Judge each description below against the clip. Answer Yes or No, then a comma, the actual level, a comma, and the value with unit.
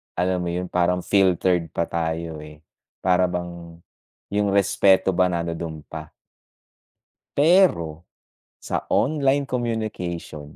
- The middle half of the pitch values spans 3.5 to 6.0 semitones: No, average, 3.0 semitones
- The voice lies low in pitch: Yes, very low, 90 Hz